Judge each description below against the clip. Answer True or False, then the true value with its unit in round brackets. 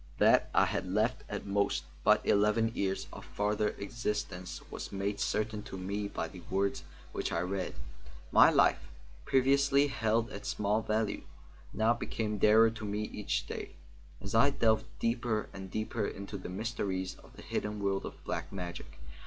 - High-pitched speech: False (105 Hz)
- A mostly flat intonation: True (2.2 semitones)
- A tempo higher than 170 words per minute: False (165 wpm)